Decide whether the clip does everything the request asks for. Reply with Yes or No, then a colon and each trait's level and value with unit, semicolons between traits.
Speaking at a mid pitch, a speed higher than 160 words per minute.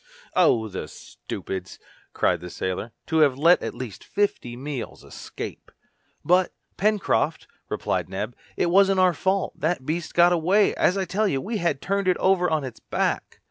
Yes: medium, 170 Hz; average, 175 wpm